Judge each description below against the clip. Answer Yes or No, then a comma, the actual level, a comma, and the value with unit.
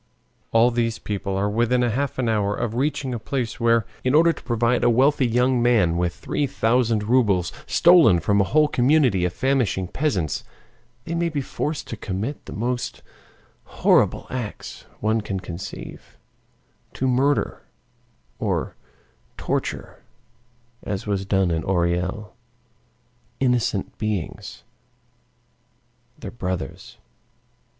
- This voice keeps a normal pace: No, slow, 125 wpm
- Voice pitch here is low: Yes, low, 115 Hz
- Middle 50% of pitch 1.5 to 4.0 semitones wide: No, average, 4.6 semitones